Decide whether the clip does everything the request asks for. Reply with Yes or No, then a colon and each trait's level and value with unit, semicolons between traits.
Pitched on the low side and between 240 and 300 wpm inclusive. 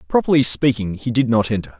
No: low, 120 Hz; average, 200 wpm